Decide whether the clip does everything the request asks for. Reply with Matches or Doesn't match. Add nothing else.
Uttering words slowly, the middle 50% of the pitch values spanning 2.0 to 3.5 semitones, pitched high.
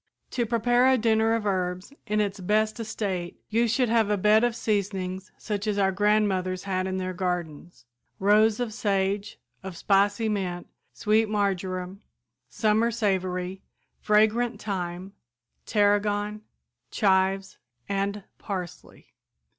Matches